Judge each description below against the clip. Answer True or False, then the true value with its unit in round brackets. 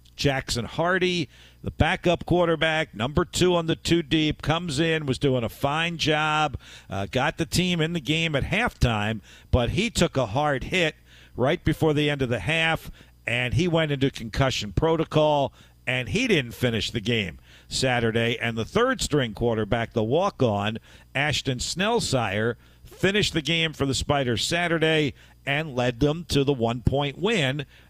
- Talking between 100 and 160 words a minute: False (170 wpm)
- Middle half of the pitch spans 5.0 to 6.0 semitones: True (5.4 semitones)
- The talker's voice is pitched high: False (140 Hz)